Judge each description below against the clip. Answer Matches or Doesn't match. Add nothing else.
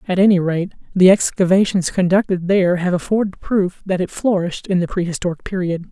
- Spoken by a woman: Matches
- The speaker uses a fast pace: Doesn't match